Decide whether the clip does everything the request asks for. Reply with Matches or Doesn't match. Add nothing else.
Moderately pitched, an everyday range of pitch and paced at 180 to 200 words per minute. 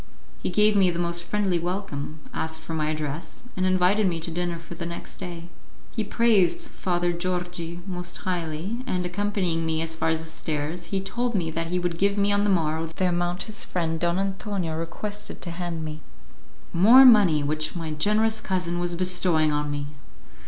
Matches